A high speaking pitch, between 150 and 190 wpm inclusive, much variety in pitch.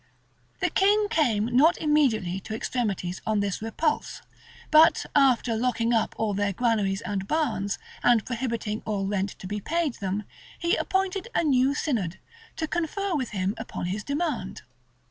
Yes: high, 230 Hz; average, 160 wpm; wide, 6.9 semitones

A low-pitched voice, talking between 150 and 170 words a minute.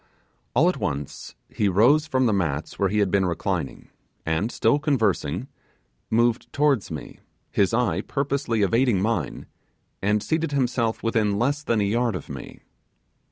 Yes: low, 115 Hz; average, 155 wpm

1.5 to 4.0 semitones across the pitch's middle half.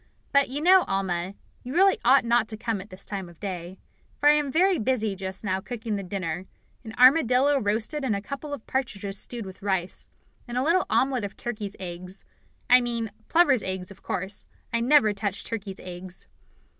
No: wide, 5.4 semitones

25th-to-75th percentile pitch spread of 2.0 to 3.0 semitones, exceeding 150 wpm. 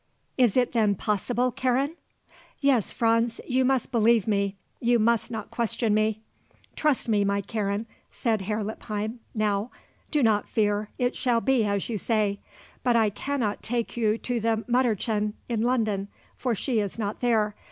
Yes: narrow, 2.6 semitones; average, 165 wpm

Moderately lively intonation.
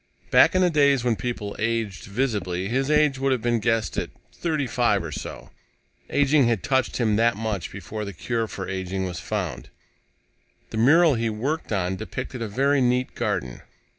Yes: average, 4.8 semitones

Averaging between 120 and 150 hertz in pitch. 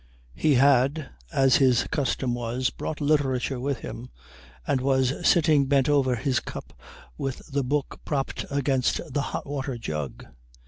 Yes: low, 135 Hz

